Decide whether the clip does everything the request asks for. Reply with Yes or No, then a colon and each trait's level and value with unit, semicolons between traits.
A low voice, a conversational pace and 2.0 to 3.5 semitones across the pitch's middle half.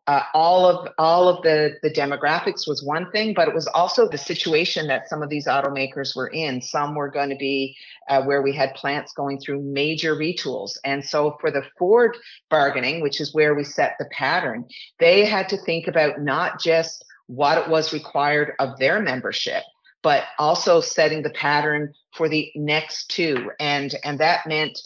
No: medium, 150 Hz; average, 190 wpm; narrow, 2.4 semitones